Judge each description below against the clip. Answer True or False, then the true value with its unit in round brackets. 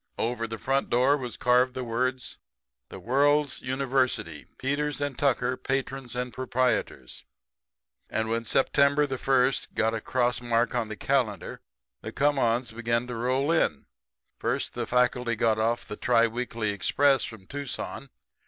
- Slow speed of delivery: False (155 wpm)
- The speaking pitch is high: False (125 Hz)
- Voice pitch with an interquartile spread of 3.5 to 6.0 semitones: False (2.6 semitones)